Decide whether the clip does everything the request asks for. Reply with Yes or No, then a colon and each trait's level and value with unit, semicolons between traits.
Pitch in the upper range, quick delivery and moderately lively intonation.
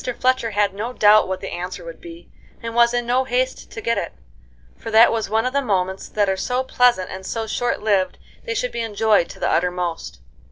Yes: high, 220 Hz; fast, 220 wpm; average, 4.4 semitones